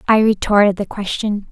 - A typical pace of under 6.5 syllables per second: Yes, 5.2 syllables/s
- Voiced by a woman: Yes, female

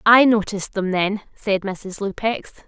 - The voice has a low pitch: No, high, 205 Hz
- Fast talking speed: No, average, 155 wpm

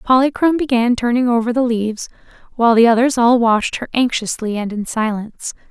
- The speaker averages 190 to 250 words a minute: No, average, 170 wpm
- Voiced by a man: No, female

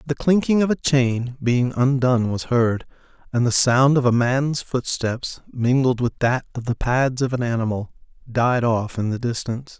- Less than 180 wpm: No, average, 185 wpm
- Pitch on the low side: Yes, low, 125 Hz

